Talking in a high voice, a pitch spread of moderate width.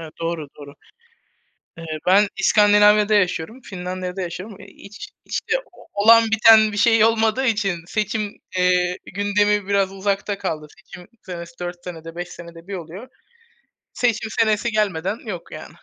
Yes: high, 200 Hz; average, 3.1 semitones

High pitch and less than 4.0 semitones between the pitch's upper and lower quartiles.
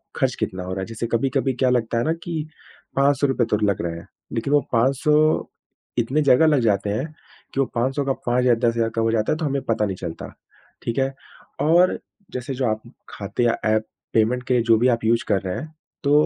No: low, 120 Hz; average, 3.5 semitones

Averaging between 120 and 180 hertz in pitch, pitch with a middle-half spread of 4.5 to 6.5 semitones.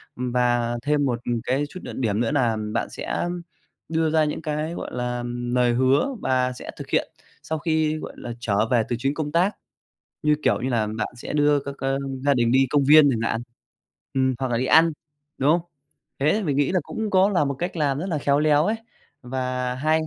No: medium, 140 Hz; average, 4.0 semitones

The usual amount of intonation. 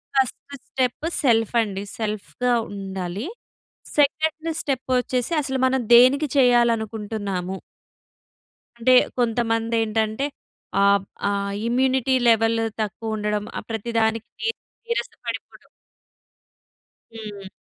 Yes: average, 3.5 semitones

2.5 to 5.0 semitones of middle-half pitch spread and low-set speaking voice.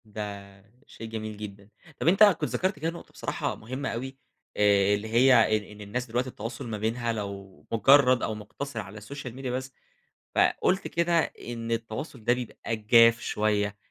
Yes: average, 3.5 semitones; low, 115 Hz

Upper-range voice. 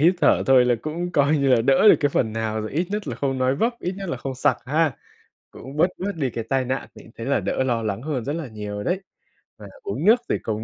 No: low, 135 Hz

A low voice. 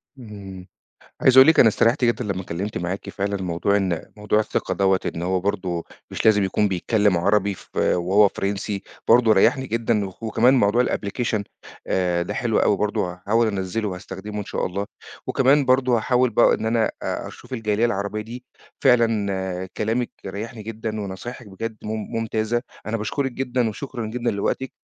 Yes: low, 105 Hz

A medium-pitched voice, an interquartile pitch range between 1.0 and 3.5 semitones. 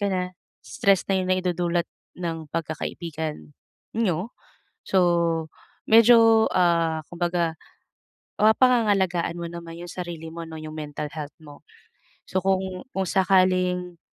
Yes: medium, 180 Hz; narrow, 2.5 semitones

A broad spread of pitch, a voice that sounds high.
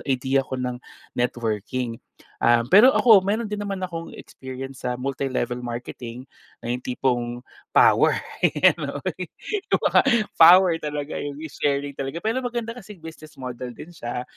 No: wide, 5.9 semitones; low, 135 Hz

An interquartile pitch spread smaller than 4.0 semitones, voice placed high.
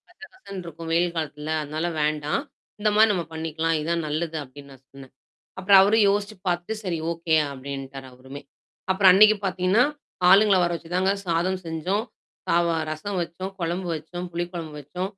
No: average, 3.5 semitones; medium, 170 Hz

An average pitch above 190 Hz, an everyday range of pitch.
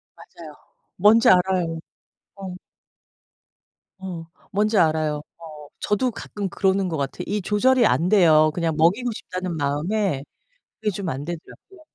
No: medium, 185 Hz; average, 4.6 semitones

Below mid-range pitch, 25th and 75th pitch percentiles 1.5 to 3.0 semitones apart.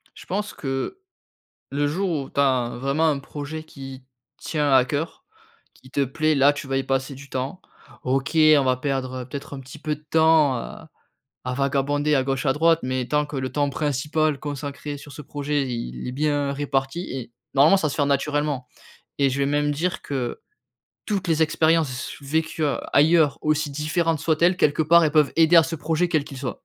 No: medium, 145 Hz; narrow, 2.5 semitones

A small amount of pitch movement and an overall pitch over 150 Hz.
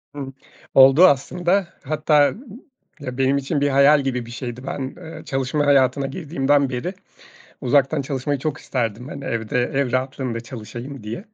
No: narrow, 2.3 semitones; low, 135 Hz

